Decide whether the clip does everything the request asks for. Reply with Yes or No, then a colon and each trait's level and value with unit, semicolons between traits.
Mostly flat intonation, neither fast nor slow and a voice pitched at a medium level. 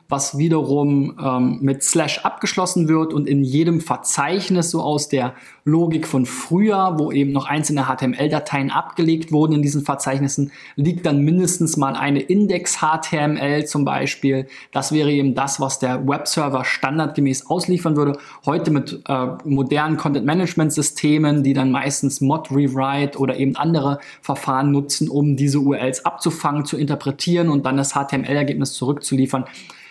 Yes: narrow, 2.3 semitones; average, 145 wpm; medium, 145 Hz